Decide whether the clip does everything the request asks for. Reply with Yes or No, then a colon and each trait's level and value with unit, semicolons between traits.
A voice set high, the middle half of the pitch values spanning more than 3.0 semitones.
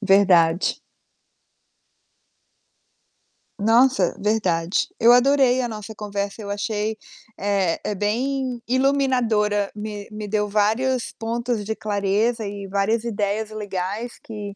No: high, 210 Hz; average, 2.7 semitones